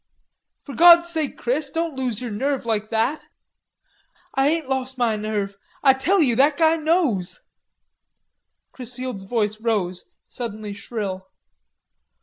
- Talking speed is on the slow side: Yes, slow, 130 wpm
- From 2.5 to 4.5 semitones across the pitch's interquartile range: No, average, 5.3 semitones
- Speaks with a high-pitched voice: Yes, very high, 250 Hz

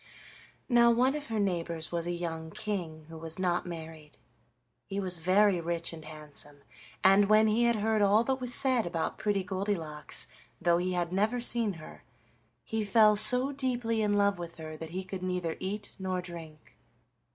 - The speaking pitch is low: No, medium, 185 Hz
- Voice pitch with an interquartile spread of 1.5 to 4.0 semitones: No, average, 4.4 semitones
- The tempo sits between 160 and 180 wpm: Yes, average, 175 wpm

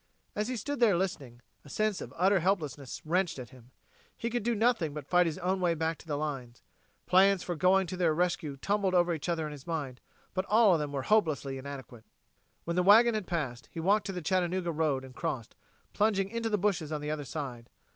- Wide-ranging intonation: No, average, 5.0 semitones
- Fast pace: Yes, fast, 225 wpm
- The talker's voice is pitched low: No, medium, 175 Hz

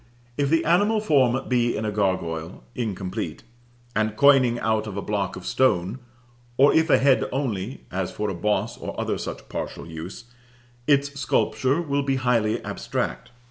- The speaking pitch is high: No, low, 120 Hz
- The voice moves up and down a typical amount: No, wide, 5.7 semitones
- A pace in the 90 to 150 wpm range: No, average, 165 wpm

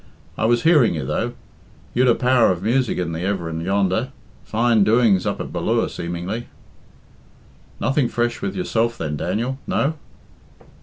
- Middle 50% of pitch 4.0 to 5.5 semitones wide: Yes, average, 5.2 semitones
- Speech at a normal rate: Yes, average, 150 wpm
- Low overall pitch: Yes, low, 115 Hz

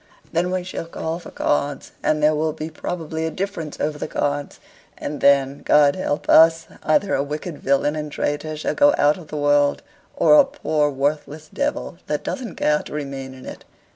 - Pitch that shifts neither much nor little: No, narrow, 2.2 semitones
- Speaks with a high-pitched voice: No, medium, 150 Hz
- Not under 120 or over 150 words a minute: No, average, 195 wpm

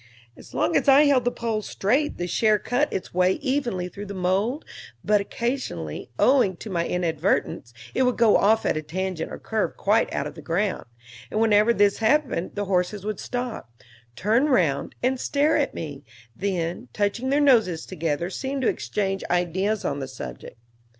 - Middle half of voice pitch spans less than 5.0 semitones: No, wide, 5.6 semitones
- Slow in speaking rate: No, average, 180 wpm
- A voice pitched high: Yes, high, 205 Hz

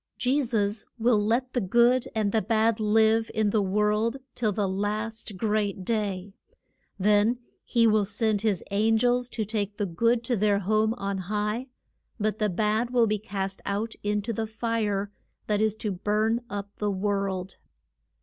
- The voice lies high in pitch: Yes, high, 215 Hz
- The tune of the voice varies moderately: No, narrow, 1.8 semitones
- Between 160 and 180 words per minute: Yes, average, 170 wpm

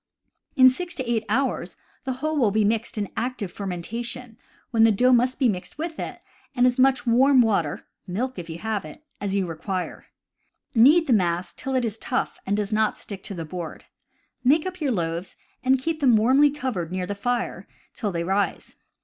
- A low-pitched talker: No, high, 230 Hz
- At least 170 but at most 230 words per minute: Yes, average, 195 wpm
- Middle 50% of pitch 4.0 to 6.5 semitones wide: Yes, average, 4.9 semitones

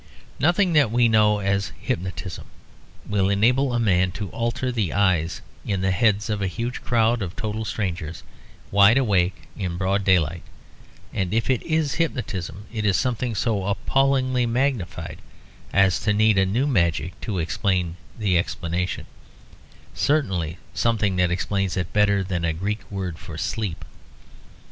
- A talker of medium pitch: No, low, 100 Hz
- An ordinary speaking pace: Yes, average, 150 wpm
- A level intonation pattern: No, average, 4.1 semitones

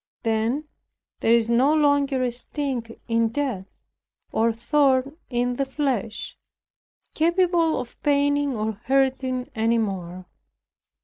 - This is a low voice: No, very high, 255 Hz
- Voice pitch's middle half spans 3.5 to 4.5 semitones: Yes, average, 3.9 semitones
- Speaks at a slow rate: Yes, slow, 115 wpm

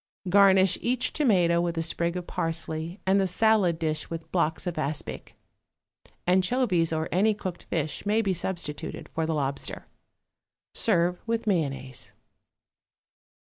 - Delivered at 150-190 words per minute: No, slow, 135 wpm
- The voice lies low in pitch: No, medium, 175 Hz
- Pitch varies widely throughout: No, average, 3.3 semitones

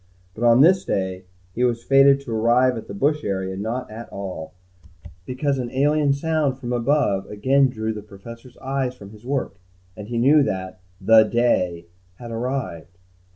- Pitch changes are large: No, average, 4.9 semitones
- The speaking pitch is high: No, low, 120 Hz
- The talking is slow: No, average, 170 wpm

